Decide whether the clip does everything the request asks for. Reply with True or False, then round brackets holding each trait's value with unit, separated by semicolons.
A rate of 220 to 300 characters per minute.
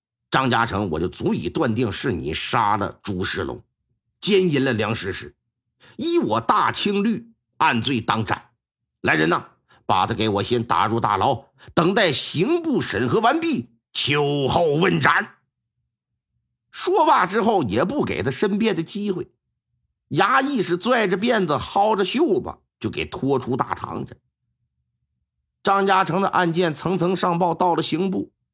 False (210 characters per minute)